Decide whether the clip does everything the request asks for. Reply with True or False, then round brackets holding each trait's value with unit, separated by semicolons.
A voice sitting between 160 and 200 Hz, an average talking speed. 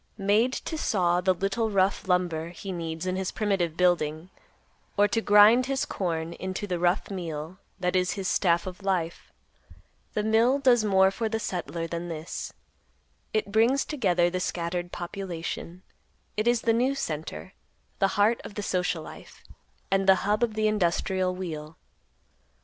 True (190 Hz; 160 wpm)